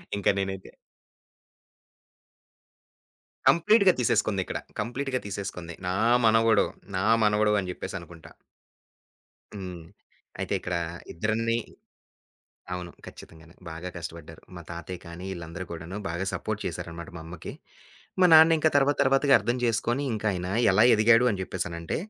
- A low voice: Yes, very low, 95 Hz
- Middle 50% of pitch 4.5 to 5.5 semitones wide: Yes, average, 4.9 semitones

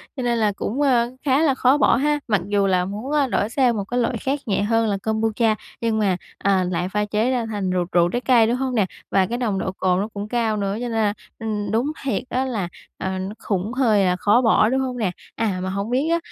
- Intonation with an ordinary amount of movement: Yes, average, 3.8 semitones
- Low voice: No, high, 220 Hz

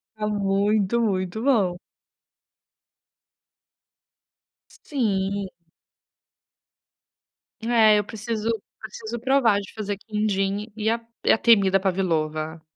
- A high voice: Yes, high, 210 Hz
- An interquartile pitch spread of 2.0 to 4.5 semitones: Yes, narrow, 2.4 semitones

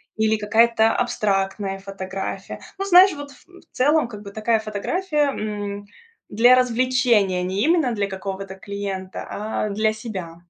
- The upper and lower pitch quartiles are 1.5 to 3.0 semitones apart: No, average, 4.1 semitones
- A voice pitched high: Yes, high, 215 Hz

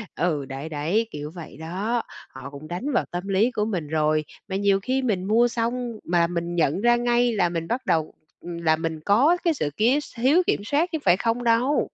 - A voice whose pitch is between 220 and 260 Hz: No, high, 195 Hz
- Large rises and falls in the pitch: Yes, wide, 6.6 semitones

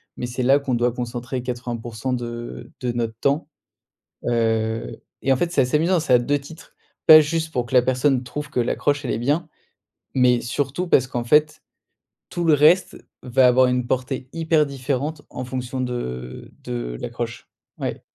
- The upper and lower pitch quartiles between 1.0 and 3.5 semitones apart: Yes, average, 3.1 semitones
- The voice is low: Yes, low, 125 Hz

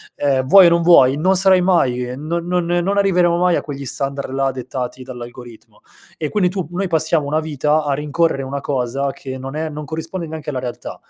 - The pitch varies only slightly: No, average, 4.4 semitones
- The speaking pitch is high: No, medium, 150 Hz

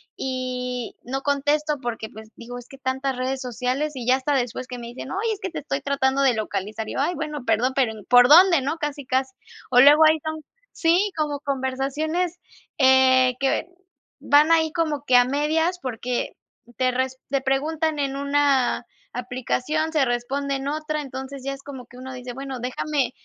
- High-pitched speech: Yes, very high, 270 Hz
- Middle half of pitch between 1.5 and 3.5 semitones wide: Yes, average, 2.9 semitones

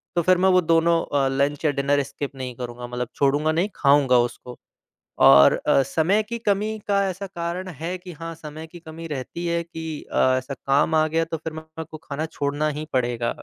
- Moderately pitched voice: Yes, medium, 155 Hz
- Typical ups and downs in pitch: Yes, average, 3.5 semitones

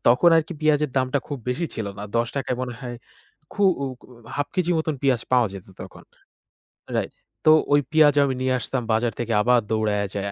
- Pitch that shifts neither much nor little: Yes, average, 3.9 semitones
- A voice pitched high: No, low, 130 Hz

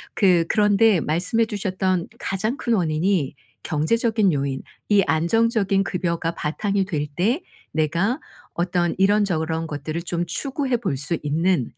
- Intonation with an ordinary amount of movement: Yes, average, 4.4 semitones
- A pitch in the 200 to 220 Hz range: No, medium, 185 Hz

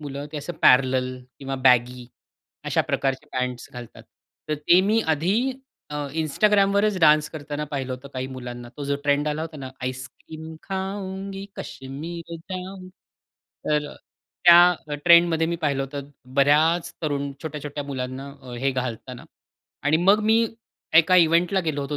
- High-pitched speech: No, medium, 150 Hz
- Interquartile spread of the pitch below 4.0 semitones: No, average, 4.4 semitones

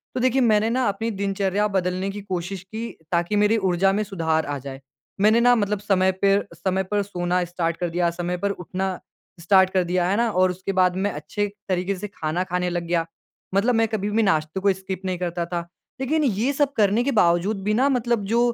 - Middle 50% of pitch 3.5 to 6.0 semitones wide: No, average, 2.9 semitones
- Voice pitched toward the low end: No, high, 190 Hz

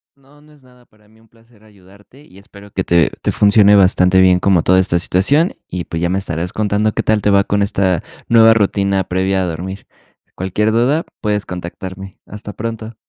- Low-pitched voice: Yes, low, 100 Hz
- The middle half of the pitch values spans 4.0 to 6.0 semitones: No, average, 2.8 semitones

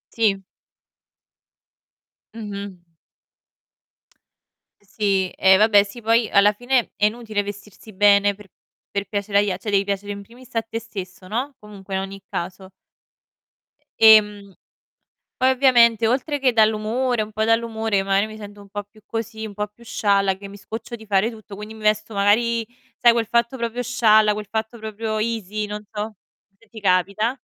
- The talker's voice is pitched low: No, high, 215 Hz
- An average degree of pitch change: No, narrow, 2.1 semitones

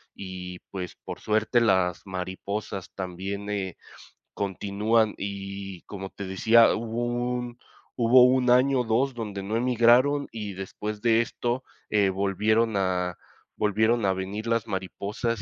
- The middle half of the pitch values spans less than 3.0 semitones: No, average, 3.3 semitones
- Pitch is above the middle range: No, low, 105 Hz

